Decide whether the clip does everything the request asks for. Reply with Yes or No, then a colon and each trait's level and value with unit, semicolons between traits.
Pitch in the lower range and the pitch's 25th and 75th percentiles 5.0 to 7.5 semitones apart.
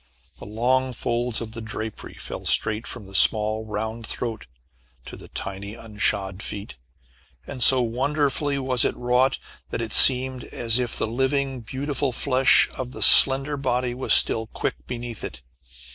No: low, 120 Hz; average, 3.0 semitones